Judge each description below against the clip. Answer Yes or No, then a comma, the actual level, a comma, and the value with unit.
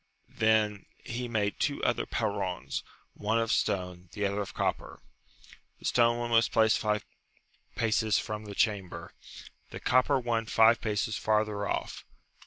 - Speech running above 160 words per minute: No, average, 145 wpm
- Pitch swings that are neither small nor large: No, narrow, 2.0 semitones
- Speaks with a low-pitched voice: Yes, low, 110 Hz